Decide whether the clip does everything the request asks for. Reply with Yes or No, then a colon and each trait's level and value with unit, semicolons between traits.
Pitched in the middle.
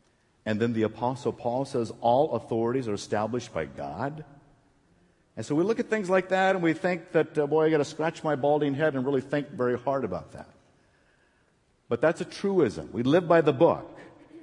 Yes: medium, 145 Hz